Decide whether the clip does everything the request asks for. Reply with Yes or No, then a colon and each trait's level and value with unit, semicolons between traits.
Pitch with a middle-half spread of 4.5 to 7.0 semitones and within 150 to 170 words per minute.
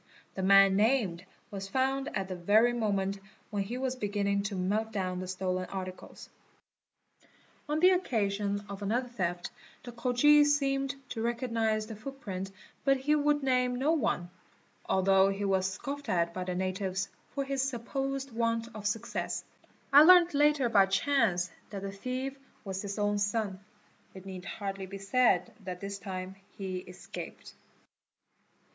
Yes: average, 5.1 semitones; average, 155 wpm